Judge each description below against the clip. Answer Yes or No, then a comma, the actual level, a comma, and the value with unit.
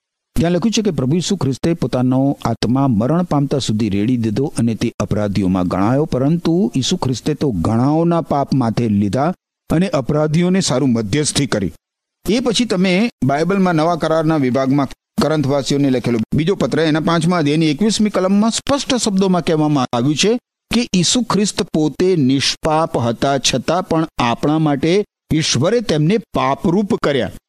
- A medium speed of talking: No, fast, 145 wpm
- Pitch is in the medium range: Yes, medium, 150 Hz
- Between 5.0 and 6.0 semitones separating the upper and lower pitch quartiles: Yes, wide, 5.6 semitones